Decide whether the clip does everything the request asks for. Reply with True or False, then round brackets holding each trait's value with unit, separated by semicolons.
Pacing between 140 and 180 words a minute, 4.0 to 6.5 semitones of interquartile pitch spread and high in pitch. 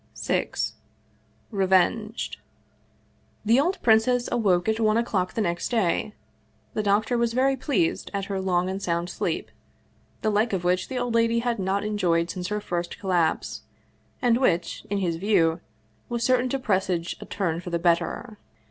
True (165 wpm; 4.5 semitones; 205 Hz)